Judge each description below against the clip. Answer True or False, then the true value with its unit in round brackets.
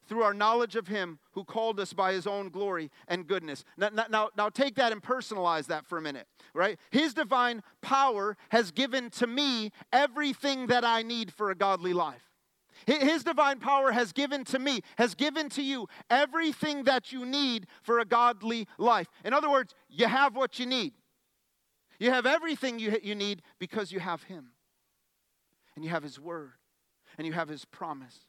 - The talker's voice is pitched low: False (230 Hz)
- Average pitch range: False (5.8 semitones)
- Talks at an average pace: True (185 wpm)